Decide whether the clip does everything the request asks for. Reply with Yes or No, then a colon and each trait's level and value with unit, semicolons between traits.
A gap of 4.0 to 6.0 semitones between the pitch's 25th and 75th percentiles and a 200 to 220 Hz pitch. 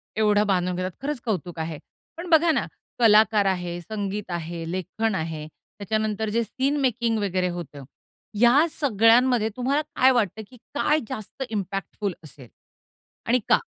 Yes: average, 4.9 semitones; high, 210 Hz